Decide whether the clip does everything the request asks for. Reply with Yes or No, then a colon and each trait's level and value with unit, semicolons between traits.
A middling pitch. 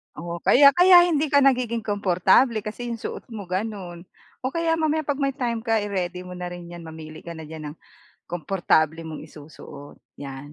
No: high, 195 Hz